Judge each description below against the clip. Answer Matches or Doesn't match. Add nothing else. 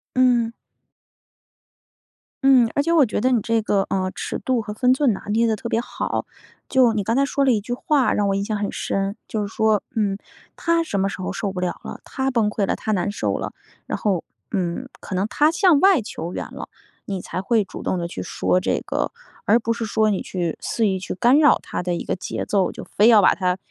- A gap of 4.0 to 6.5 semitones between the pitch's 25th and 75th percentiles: Matches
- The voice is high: Matches